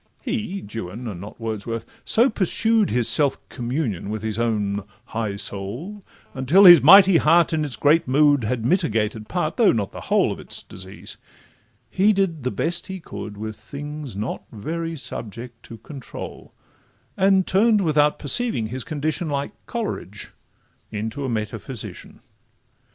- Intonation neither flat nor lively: No, wide, 7.8 semitones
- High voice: No, low, 135 Hz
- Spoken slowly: No, average, 150 wpm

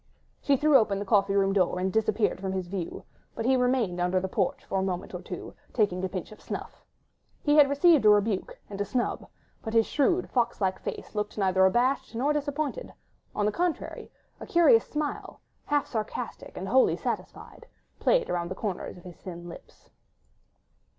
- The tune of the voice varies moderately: No, wide, 6.0 semitones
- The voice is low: No, high, 210 Hz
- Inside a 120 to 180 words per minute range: No, average, 190 wpm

